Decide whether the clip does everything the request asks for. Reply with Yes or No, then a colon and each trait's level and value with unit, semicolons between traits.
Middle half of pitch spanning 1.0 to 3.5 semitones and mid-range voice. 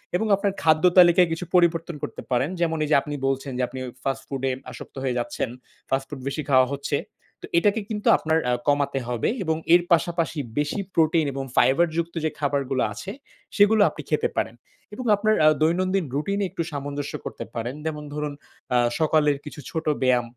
No: average, 4.0 semitones; medium, 155 Hz